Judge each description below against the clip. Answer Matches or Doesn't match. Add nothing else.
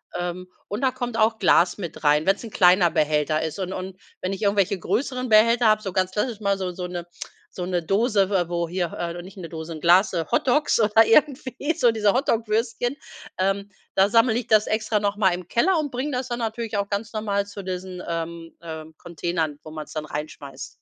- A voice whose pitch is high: Matches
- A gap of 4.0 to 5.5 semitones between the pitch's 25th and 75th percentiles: Matches